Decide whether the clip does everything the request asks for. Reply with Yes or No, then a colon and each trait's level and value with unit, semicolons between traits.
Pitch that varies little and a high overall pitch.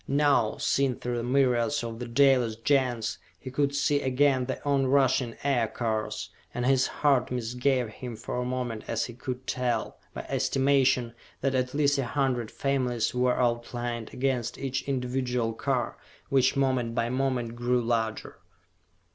No: narrow, 2.2 semitones; low, 125 Hz